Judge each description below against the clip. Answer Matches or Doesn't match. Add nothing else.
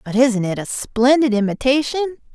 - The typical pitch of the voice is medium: Doesn't match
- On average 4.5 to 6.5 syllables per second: Matches